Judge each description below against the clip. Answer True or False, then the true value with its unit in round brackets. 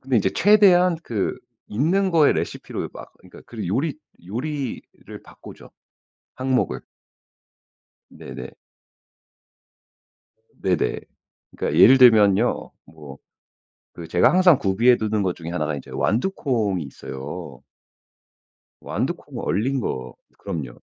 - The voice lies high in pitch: False (110 Hz)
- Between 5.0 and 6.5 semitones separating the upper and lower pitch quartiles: False (7.7 semitones)